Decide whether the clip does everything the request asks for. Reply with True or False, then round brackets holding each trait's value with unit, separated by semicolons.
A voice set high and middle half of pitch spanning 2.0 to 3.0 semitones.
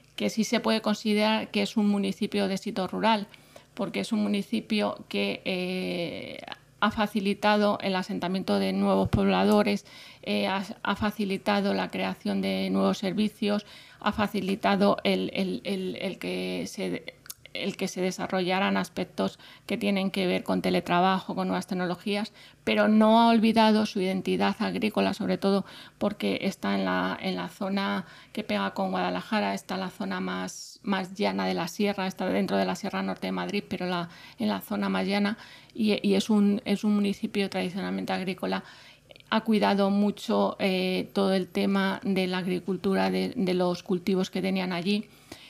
True (195 Hz; 2.4 semitones)